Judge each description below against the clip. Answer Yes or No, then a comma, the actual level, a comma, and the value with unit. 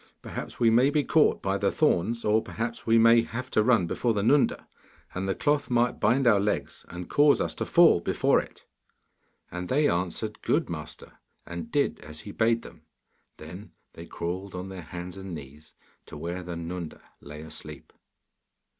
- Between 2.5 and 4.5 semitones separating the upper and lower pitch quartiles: No, average, 5.2 semitones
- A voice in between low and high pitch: No, low, 100 Hz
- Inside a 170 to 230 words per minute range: Yes, average, 180 wpm